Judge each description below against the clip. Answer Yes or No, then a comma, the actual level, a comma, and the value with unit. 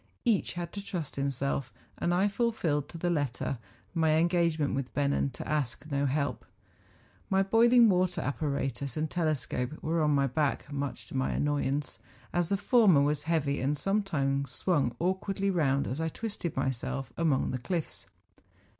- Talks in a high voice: No, medium, 155 Hz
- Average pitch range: Yes, average, 4.3 semitones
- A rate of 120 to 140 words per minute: No, average, 165 wpm